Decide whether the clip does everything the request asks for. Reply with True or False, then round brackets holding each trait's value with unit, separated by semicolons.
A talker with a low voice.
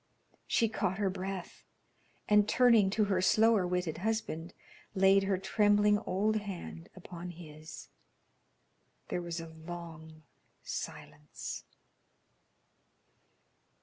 False (190 Hz)